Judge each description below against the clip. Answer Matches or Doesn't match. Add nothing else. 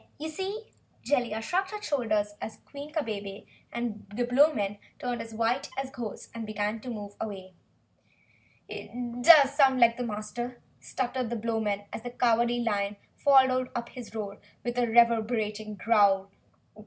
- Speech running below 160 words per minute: Matches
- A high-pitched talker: Matches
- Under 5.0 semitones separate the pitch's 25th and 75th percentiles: Matches